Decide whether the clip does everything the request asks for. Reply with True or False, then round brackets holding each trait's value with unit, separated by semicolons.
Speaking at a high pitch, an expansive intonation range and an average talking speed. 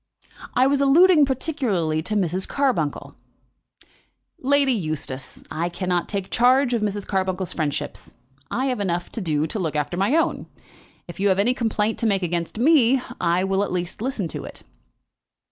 True (200 Hz; 6.6 semitones; 165 wpm)